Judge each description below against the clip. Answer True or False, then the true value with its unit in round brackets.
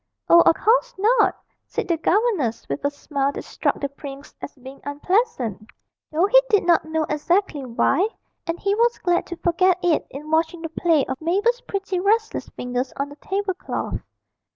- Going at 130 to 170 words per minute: False (180 wpm)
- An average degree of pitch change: False (5.8 semitones)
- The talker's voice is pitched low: False (340 Hz)